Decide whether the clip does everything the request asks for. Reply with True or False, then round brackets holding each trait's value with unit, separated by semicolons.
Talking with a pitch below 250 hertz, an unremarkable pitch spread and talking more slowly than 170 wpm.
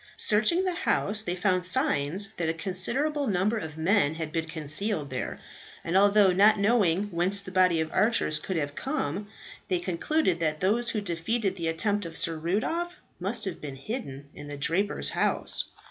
False (185 Hz; 4.5 semitones; 175 wpm)